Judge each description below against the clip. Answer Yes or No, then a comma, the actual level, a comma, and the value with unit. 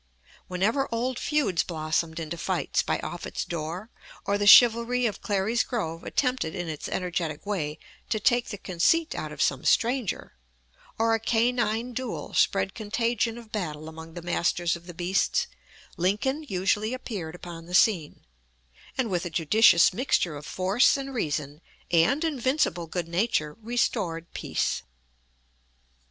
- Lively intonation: Yes, wide, 5.8 semitones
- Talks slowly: No, average, 145 wpm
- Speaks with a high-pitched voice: Yes, high, 195 Hz